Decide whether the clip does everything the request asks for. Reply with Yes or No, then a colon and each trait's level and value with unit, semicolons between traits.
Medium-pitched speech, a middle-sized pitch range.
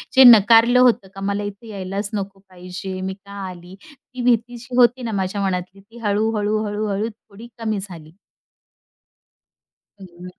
No: high, 205 Hz; average, 3.1 semitones